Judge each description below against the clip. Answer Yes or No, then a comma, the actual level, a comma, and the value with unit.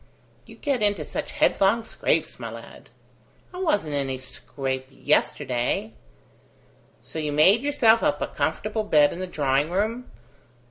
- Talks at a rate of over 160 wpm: No, average, 145 wpm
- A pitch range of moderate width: No, wide, 7.7 semitones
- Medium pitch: Yes, medium, 160 Hz